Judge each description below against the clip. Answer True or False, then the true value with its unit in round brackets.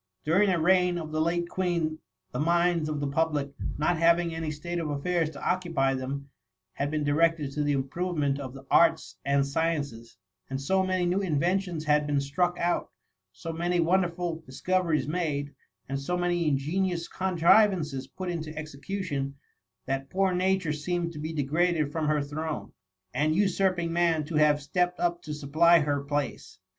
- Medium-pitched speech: True (160 Hz)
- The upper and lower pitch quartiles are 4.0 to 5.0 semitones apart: False (3.3 semitones)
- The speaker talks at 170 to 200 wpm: True (175 wpm)